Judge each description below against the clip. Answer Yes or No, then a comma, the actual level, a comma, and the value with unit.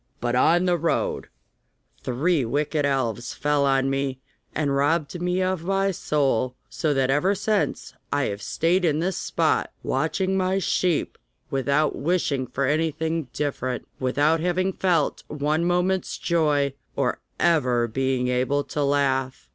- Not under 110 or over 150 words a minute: Yes, average, 145 wpm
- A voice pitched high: No, medium, 150 Hz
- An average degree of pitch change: Yes, average, 4.5 semitones